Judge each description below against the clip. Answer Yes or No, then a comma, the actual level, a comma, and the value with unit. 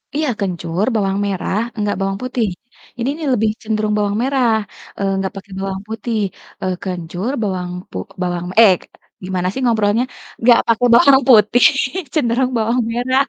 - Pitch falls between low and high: No, high, 215 Hz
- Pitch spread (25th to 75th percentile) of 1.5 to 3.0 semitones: No, average, 3.9 semitones